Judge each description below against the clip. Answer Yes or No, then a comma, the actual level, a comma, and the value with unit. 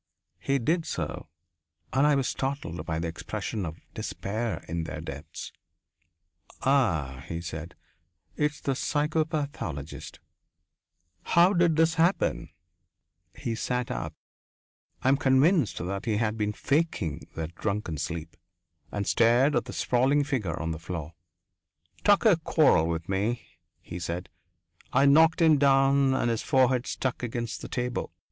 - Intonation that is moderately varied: No, wide, 8.8 semitones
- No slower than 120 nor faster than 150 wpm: Yes, average, 140 wpm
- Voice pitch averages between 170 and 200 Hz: No, low, 120 Hz